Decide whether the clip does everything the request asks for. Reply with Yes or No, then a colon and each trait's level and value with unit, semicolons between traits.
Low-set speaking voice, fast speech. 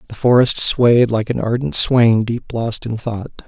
No: low, 115 Hz; average, 190 wpm